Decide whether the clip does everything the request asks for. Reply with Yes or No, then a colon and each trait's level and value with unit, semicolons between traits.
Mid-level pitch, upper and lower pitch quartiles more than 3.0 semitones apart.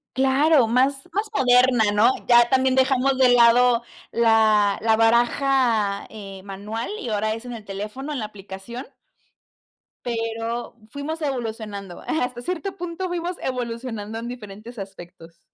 No: high, 235 Hz; average, 3.6 semitones